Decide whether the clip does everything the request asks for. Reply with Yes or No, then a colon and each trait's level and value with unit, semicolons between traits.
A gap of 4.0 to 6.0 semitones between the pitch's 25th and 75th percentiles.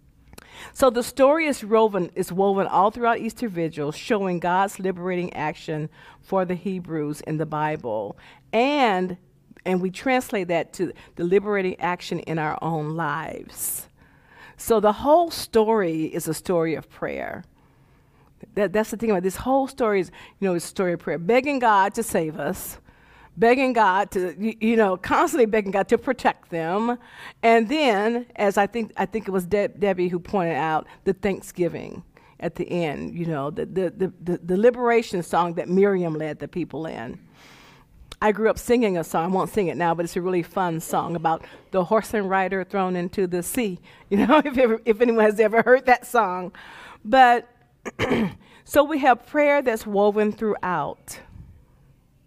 Yes: average, 4.7 semitones